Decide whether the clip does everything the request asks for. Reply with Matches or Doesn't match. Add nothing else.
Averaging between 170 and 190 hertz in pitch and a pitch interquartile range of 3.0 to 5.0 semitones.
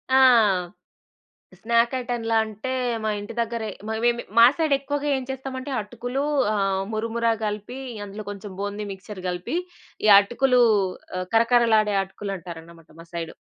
Doesn't match